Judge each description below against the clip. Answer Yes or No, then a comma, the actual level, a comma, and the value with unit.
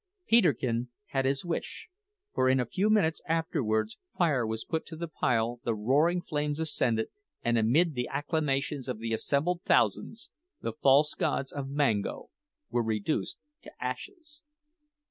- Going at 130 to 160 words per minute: Yes, average, 145 wpm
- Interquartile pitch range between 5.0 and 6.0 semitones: Yes, wide, 5.5 semitones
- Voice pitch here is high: No, medium, 140 Hz